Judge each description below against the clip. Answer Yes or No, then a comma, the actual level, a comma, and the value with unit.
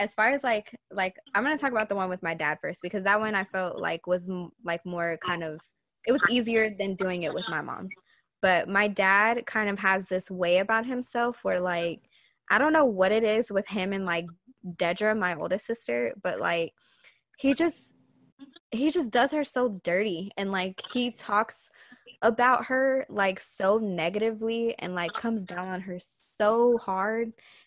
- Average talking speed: Yes, average, 195 wpm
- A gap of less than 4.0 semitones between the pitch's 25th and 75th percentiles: No, average, 4.6 semitones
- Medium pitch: No, high, 205 Hz